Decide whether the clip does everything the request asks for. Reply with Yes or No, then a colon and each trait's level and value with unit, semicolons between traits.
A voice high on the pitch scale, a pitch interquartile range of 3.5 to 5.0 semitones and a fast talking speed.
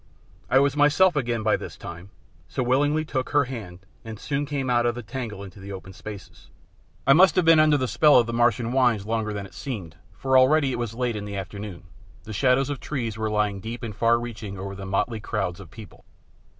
No: low, 115 Hz; average, 4.5 semitones; fast, 225 wpm